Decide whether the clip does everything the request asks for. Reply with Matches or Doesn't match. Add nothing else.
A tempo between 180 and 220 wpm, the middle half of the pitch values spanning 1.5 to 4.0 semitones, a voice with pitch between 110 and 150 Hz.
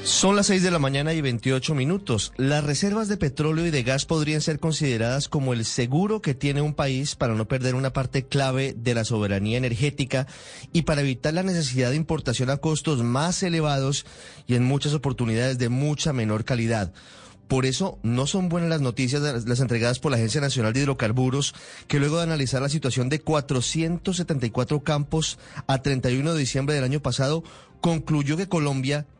Matches